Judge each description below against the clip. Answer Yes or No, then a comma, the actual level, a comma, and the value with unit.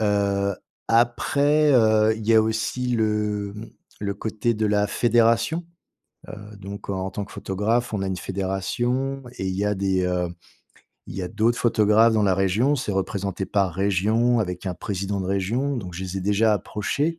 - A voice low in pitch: Yes, low, 105 Hz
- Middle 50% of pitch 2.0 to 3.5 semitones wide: Yes, average, 3.0 semitones